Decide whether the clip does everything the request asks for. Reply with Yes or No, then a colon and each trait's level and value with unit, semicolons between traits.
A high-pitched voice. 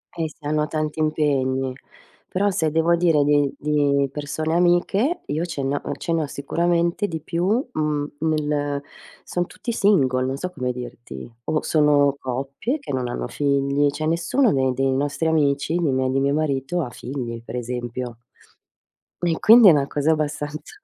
No: medium, 150 Hz